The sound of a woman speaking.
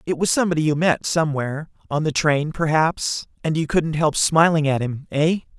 No: male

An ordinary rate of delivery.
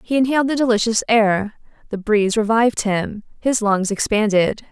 Yes: average, 155 wpm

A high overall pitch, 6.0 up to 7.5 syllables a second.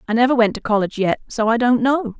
Yes: high, 230 Hz; 6.6 syllables/s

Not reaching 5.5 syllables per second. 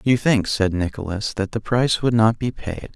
Yes: 5.0 syllables/s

